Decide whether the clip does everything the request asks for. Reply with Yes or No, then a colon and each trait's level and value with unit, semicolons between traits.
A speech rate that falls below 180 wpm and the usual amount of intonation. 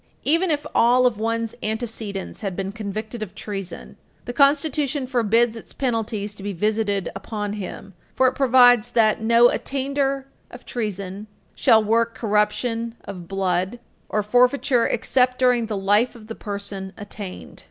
Yes: average, 150 wpm; average, 3.3 semitones